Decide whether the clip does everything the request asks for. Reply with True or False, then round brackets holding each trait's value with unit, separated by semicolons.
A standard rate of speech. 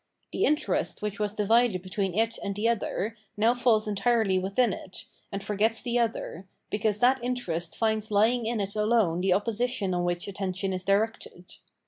True (170 wpm)